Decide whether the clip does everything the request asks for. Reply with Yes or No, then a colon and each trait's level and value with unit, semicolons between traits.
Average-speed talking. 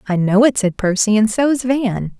No: fast, 220 wpm